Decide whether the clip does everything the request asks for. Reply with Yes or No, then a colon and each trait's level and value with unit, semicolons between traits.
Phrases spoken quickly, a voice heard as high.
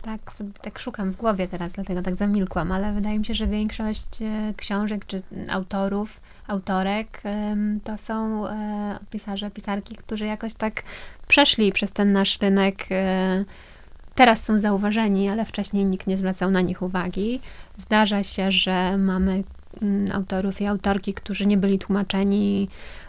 No: average, 140 wpm; high, 200 Hz